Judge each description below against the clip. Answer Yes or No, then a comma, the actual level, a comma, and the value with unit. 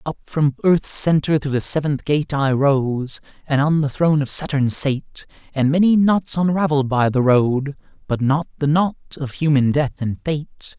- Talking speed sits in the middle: Yes, average, 185 wpm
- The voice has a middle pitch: Yes, medium, 145 Hz